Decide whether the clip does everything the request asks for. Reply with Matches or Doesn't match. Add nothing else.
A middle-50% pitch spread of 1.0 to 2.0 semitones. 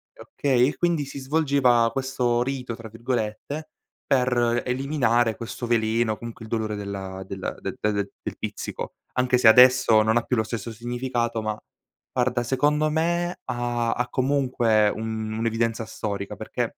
Doesn't match